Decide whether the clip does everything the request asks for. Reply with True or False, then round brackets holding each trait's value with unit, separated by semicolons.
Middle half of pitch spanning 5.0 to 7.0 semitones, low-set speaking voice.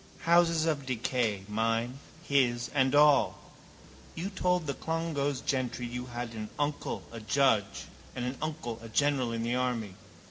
False (3.8 semitones; 130 Hz)